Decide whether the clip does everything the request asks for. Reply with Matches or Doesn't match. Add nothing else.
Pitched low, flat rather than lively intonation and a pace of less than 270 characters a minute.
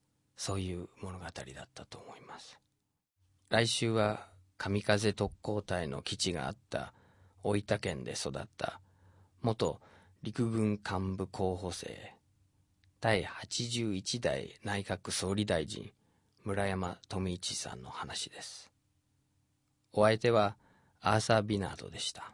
Matches